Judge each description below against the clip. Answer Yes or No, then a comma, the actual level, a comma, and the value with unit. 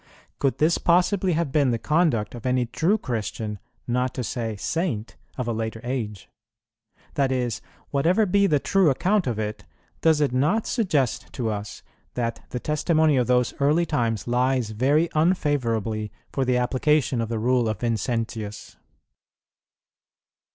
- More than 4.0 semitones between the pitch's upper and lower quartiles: Yes, average, 5.1 semitones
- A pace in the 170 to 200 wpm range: No, average, 155 wpm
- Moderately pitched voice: No, low, 125 Hz